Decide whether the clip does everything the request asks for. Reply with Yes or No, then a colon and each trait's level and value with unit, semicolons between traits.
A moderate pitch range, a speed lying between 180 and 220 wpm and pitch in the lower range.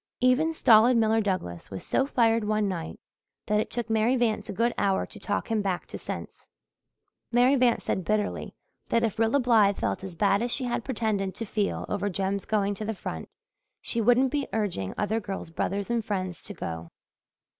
No: average, 3.1 semitones; average, 195 wpm; high, 215 Hz